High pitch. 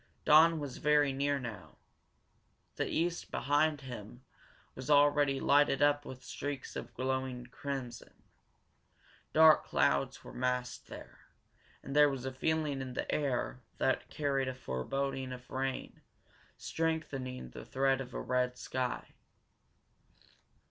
No: low, 135 Hz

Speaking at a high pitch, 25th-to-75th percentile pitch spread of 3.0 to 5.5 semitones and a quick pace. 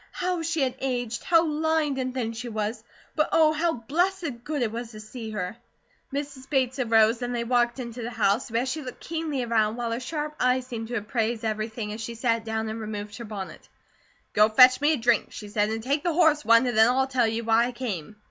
Yes: high, 240 Hz; average, 3.5 semitones; fast, 230 wpm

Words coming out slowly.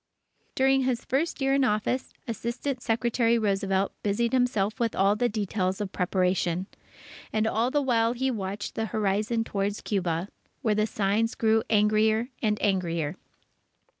No: average, 145 wpm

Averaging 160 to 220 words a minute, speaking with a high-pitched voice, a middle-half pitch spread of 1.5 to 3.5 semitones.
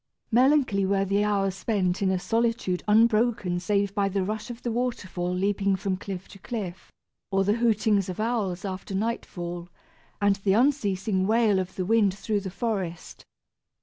Yes: average, 165 wpm; high, 200 Hz; average, 2.9 semitones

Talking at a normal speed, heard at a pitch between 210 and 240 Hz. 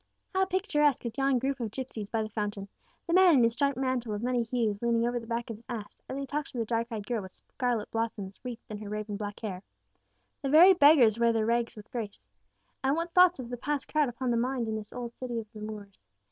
No: fast, 250 wpm; high, 235 Hz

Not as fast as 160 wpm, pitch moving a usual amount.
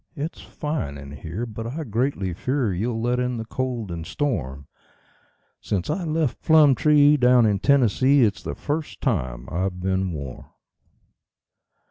No: average, 145 wpm; wide, 7.3 semitones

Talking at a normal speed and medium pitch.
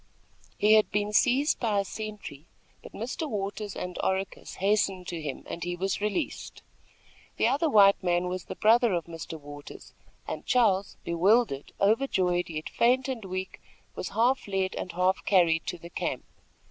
No: average, 165 wpm; high, 195 Hz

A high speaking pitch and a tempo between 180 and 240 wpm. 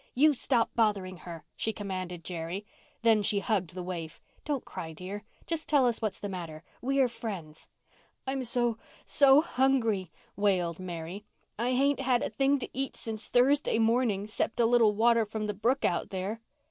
No: high, 220 Hz; average, 165 wpm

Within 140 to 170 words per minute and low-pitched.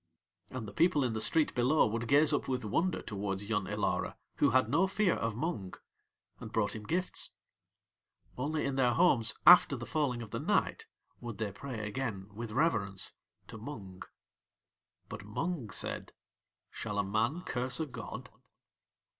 Yes: average, 165 wpm; low, 120 Hz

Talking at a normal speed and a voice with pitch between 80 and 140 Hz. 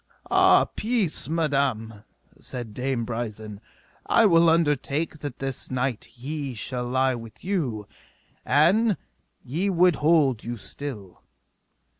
No: slow, 115 wpm; low, 135 Hz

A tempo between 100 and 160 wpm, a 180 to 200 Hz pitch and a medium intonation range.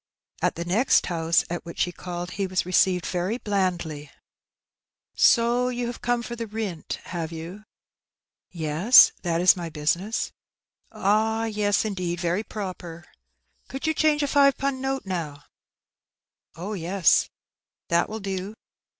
Yes: average, 145 wpm; high, 190 Hz; average, 4.6 semitones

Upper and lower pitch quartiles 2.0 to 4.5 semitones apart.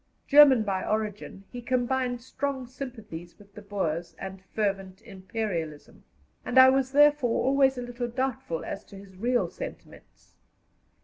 No: average, 5.0 semitones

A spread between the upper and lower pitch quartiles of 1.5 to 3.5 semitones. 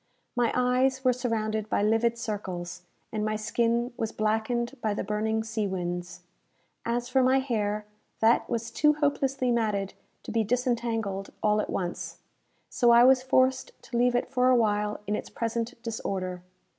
Yes: average, 2.8 semitones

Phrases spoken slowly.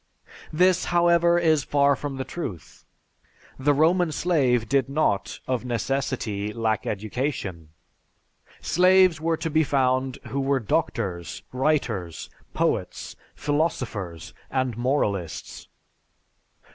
Yes: slow, 105 wpm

